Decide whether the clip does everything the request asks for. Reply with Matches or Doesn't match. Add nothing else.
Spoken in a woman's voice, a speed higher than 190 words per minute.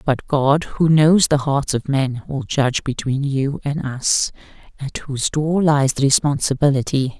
Doesn't match